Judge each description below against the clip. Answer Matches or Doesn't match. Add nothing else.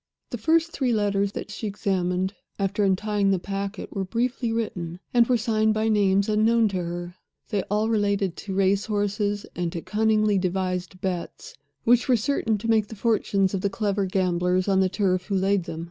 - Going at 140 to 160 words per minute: Doesn't match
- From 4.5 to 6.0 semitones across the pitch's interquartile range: Doesn't match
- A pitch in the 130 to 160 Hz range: Doesn't match